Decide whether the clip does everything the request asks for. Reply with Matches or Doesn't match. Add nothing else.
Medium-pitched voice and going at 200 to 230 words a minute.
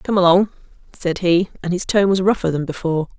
Matches